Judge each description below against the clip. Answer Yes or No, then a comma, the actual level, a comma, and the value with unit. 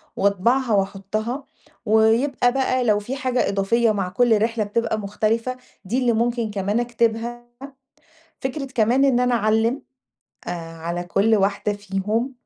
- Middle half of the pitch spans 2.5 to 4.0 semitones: Yes, average, 3.1 semitones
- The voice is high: Yes, high, 225 Hz